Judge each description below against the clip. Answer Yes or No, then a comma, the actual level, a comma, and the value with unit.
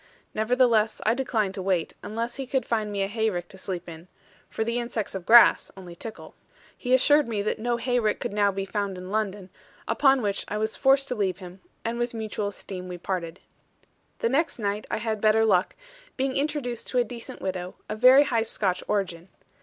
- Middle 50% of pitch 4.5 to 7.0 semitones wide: No, average, 3.8 semitones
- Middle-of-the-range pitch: No, high, 215 Hz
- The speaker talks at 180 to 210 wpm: Yes, average, 200 wpm